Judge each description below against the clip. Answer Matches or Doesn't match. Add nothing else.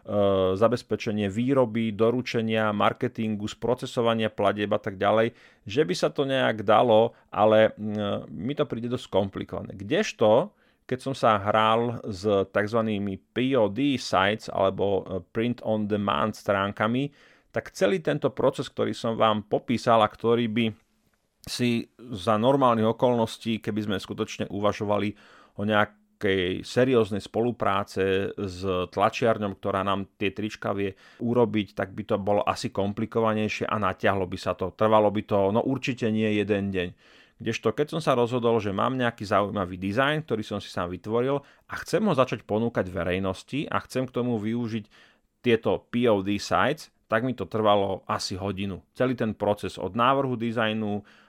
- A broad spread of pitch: Doesn't match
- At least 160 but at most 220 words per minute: Doesn't match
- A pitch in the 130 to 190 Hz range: Doesn't match